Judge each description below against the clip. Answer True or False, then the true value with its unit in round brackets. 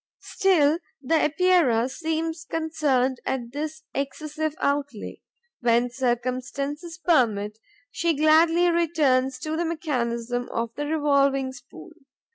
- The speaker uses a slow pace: True (105 wpm)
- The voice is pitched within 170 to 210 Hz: False (290 Hz)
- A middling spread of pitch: True (4.1 semitones)